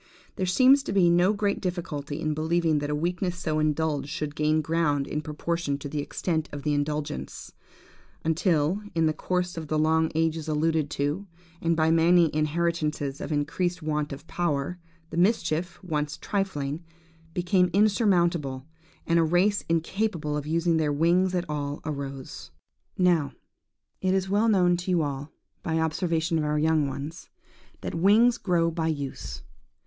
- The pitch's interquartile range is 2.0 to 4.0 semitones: Yes, average, 2.9 semitones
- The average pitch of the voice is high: No, medium, 160 Hz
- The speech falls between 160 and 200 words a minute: Yes, average, 165 wpm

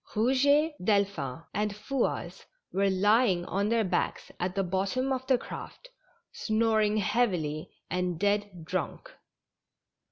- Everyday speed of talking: No, slow, 120 wpm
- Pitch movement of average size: Yes, average, 4.3 semitones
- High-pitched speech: Yes, high, 205 Hz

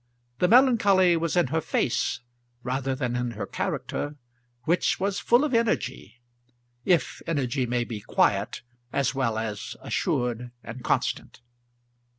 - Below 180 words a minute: Yes, slow, 135 wpm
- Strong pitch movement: Yes, wide, 6.7 semitones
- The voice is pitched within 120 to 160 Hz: Yes, low, 135 Hz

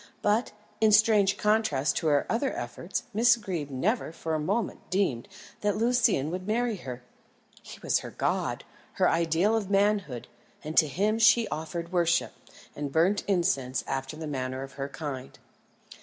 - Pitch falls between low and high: Yes, medium, 175 Hz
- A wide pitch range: Yes, wide, 6.7 semitones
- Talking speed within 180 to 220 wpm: No, average, 160 wpm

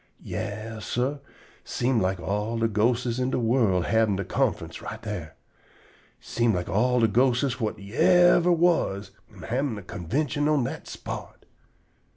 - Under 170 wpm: Yes, average, 150 wpm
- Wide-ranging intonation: No, average, 3.8 semitones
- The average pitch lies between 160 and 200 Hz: No, low, 115 Hz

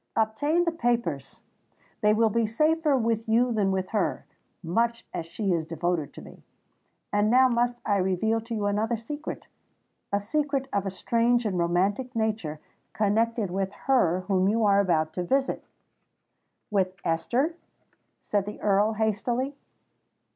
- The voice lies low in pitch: No, high, 215 Hz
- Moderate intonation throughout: Yes, average, 3.9 semitones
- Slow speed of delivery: No, average, 145 wpm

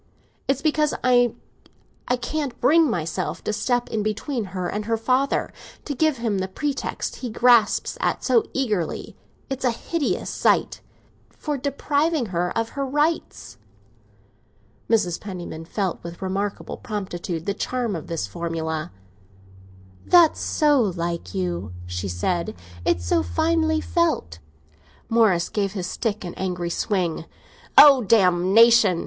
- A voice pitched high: Yes, high, 210 Hz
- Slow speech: Yes, slow, 130 wpm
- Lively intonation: Yes, wide, 6.9 semitones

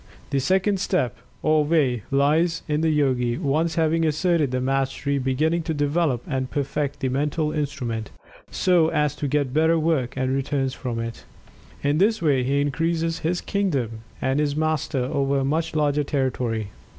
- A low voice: No, medium, 145 Hz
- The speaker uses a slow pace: No, average, 165 wpm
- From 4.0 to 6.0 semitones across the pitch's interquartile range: No, average, 3.3 semitones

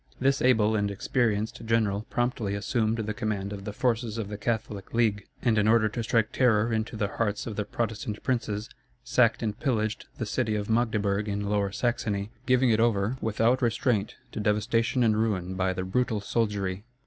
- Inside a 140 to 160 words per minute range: No, average, 185 wpm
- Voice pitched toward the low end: Yes, low, 110 Hz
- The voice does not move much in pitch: Yes, narrow, 2.3 semitones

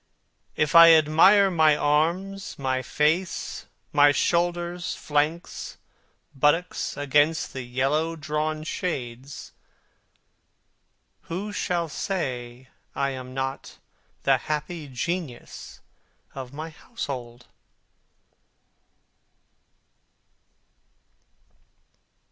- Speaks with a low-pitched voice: No, medium, 150 Hz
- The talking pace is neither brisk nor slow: No, slow, 75 wpm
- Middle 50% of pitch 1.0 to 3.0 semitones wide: No, average, 4.1 semitones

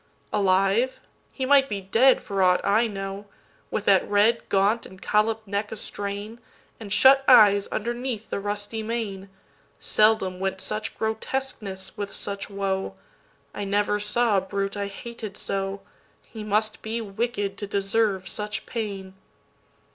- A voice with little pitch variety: Yes, narrow, 2.2 semitones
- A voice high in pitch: Yes, high, 205 Hz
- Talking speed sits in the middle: No, slow, 130 wpm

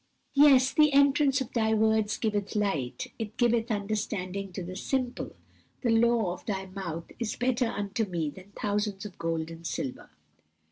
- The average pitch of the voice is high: Yes, high, 210 Hz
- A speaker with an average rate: Yes, average, 160 wpm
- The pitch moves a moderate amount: Yes, average, 4.1 semitones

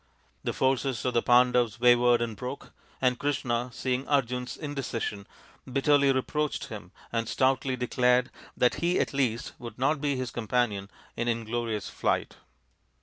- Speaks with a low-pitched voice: Yes, low, 125 Hz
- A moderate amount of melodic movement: No, narrow, 2.2 semitones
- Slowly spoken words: No, average, 145 wpm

